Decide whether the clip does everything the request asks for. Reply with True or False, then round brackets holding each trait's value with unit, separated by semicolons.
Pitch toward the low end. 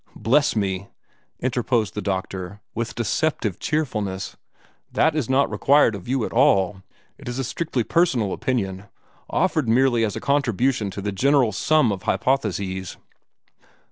True (115 Hz)